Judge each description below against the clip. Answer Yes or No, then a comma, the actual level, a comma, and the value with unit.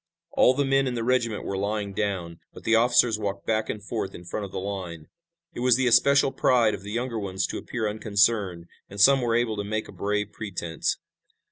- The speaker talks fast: Yes, fast, 220 wpm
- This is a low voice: Yes, low, 105 Hz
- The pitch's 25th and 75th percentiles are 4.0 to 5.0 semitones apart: No, average, 3.3 semitones